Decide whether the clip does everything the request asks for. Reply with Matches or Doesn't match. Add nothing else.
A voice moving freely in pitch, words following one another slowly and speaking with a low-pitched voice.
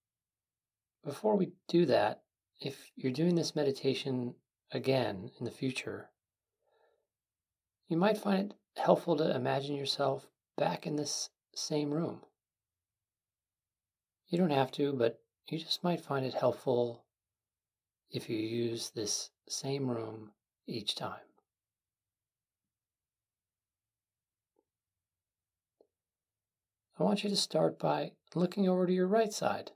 Matches